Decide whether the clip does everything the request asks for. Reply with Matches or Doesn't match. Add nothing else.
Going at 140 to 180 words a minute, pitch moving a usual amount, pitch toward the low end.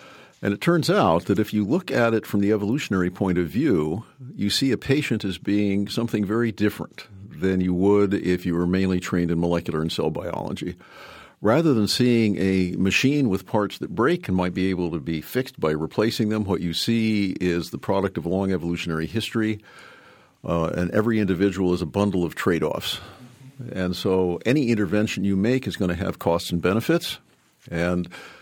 Doesn't match